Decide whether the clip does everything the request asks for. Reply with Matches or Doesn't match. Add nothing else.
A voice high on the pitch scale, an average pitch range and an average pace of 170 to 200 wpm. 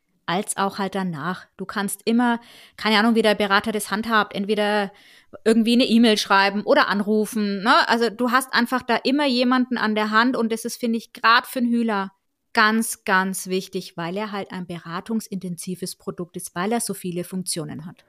Matches